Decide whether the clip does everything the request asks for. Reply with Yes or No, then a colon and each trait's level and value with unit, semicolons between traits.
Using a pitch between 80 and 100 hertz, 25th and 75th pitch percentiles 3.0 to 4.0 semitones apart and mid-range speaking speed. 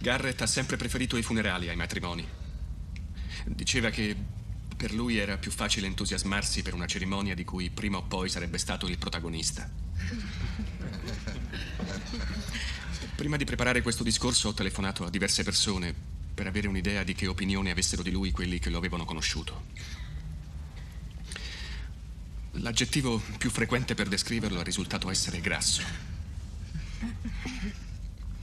Yes: very low, 95 Hz; average, 3.6 semitones; average, 130 wpm